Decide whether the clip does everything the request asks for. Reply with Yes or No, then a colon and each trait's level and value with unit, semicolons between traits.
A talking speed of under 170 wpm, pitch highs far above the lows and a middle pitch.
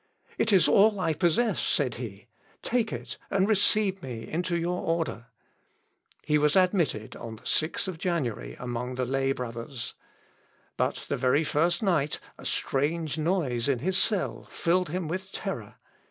Yes: average, 155 wpm; wide, 6.4 semitones; medium, 160 Hz